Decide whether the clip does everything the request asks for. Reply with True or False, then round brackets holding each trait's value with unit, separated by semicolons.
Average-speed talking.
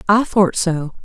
True (175 wpm)